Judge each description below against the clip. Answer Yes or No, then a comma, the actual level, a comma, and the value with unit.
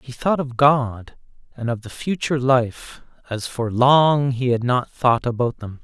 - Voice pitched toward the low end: Yes, low, 125 Hz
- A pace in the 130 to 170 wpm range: No, average, 185 wpm